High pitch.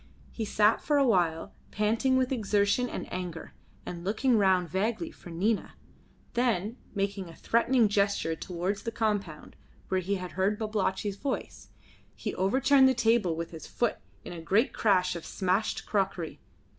Yes: high, 200 Hz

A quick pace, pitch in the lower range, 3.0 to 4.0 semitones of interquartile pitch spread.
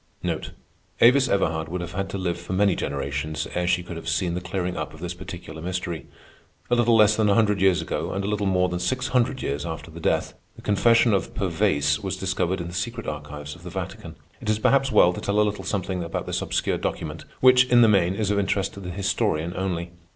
Yes: fast, 230 wpm; very low, 95 Hz; average, 3.3 semitones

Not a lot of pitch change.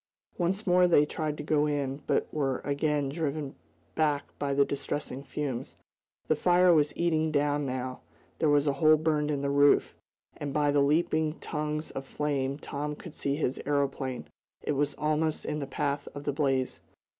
Yes: narrow, 1.6 semitones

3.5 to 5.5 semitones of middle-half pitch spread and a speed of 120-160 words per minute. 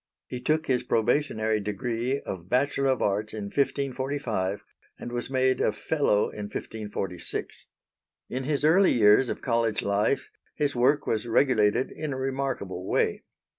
Yes: average, 4.5 semitones; average, 145 wpm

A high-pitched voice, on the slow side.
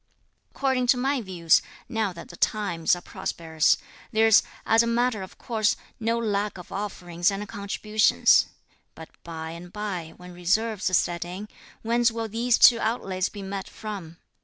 No: high, 205 Hz; average, 160 wpm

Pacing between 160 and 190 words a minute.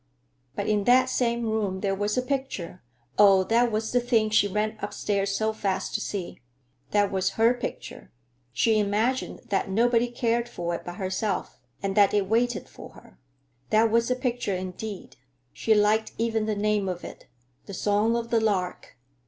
Yes: average, 175 wpm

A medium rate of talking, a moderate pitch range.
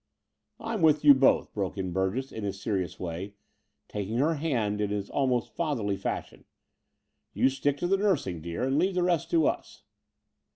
No: average, 180 wpm; wide, 7.7 semitones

